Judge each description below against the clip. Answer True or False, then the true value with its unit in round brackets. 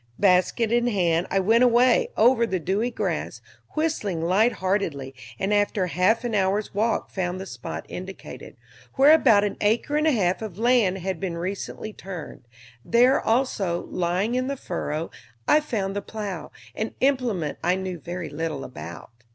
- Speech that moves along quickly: False (165 wpm)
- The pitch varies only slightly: False (4.6 semitones)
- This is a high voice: True (195 Hz)